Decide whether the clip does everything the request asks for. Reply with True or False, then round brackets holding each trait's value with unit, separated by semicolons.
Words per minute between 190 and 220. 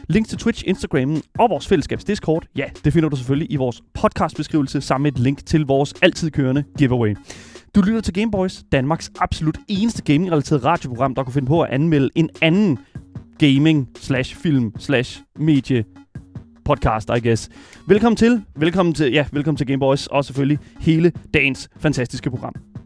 False (155 wpm)